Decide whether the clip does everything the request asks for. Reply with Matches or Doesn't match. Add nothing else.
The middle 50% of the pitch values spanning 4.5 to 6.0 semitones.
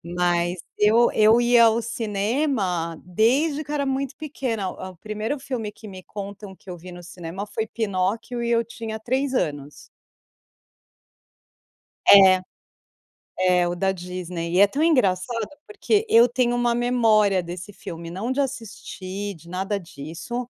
Matches